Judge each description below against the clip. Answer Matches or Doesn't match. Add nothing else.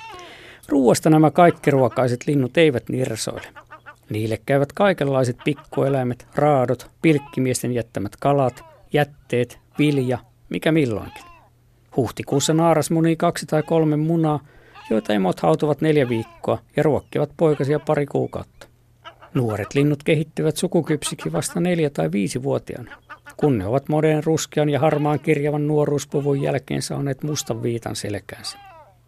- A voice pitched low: Doesn't match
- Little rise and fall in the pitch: Doesn't match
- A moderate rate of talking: Matches